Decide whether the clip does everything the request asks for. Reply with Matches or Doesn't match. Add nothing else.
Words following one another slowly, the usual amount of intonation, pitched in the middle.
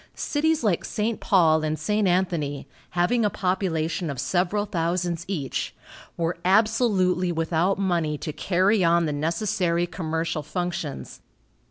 Matches